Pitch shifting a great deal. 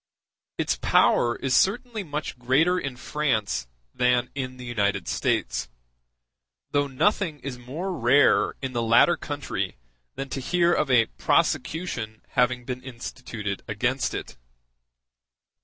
No: average, 3.8 semitones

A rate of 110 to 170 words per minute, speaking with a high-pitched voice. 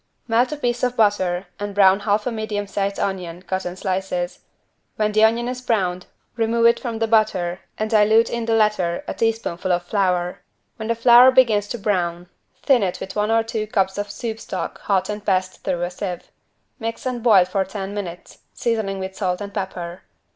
No: average, 195 wpm; high, 205 Hz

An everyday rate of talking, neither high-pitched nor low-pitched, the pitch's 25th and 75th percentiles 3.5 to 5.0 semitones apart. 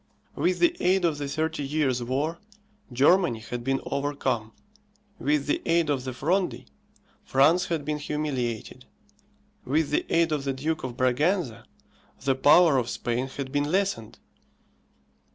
Yes: average, 145 wpm; medium, 145 Hz; average, 3.8 semitones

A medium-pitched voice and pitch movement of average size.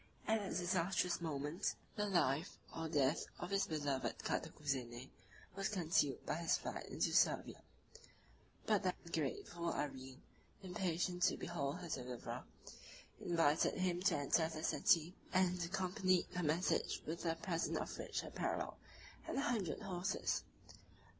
Yes: medium, 170 Hz; average, 3.7 semitones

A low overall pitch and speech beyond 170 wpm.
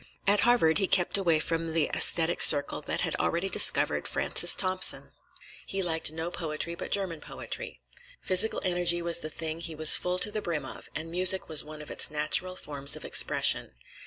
No: medium, 170 Hz; average, 190 wpm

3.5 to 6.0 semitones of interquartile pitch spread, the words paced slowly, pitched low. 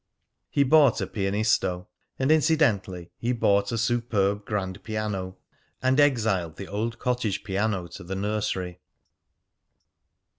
Yes: average, 3.8 semitones; slow, 120 wpm; low, 105 Hz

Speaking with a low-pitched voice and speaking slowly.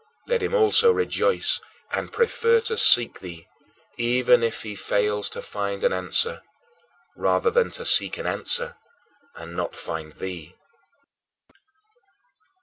Yes: low, 125 Hz; slow, 130 wpm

